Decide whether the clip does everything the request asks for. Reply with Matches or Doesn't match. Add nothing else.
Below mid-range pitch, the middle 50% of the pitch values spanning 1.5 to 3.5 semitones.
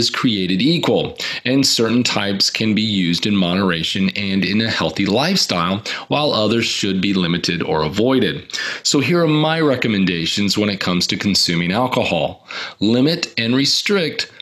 Doesn't match